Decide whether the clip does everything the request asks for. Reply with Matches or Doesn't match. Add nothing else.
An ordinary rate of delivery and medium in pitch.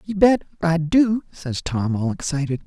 Matches